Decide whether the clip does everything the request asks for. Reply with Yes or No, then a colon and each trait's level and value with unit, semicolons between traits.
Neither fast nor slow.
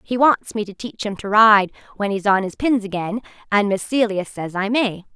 No: fast, 235 wpm